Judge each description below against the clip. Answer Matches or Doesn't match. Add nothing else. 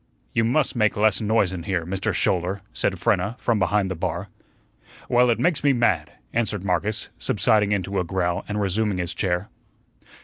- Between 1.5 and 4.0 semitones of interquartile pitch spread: Matches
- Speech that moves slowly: Doesn't match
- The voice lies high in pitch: Doesn't match